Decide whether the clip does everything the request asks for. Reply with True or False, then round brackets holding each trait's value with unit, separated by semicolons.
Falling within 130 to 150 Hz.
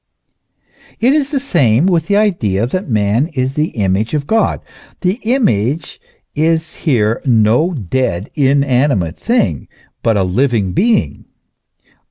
True (135 Hz)